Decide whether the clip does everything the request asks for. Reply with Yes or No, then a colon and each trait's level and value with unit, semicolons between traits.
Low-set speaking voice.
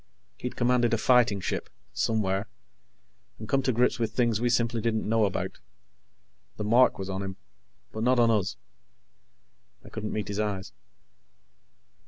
Yes: low, 110 Hz